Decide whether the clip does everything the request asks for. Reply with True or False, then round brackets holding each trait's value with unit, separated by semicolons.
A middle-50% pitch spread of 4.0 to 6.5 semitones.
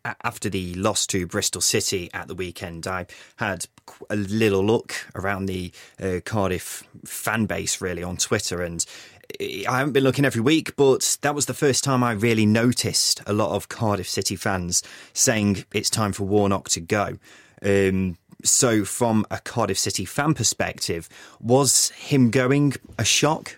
True (4.5 semitones)